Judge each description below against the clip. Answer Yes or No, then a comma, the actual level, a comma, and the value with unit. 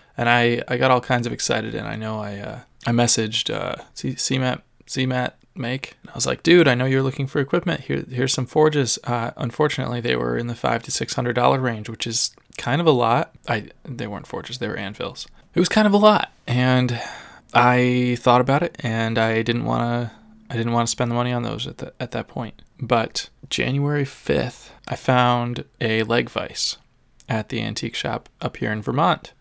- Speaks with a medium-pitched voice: No, low, 125 Hz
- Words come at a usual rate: No, fast, 210 wpm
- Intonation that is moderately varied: No, narrow, 2.1 semitones